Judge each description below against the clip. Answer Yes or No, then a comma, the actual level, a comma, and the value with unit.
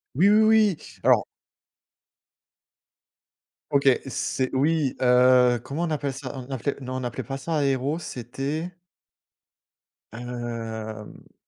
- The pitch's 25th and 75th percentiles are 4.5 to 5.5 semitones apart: No, average, 2.8 semitones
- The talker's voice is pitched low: Yes, low, 130 Hz